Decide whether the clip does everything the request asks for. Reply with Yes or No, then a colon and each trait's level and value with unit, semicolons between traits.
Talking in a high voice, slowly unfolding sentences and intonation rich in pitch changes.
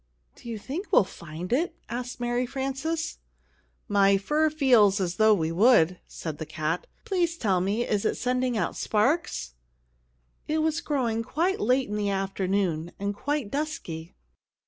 No: high, 220 Hz; average, 155 wpm; wide, 6.3 semitones